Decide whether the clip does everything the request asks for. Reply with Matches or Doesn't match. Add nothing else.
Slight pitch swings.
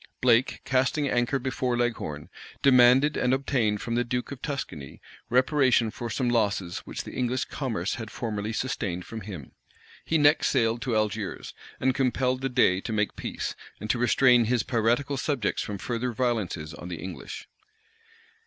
Doesn't match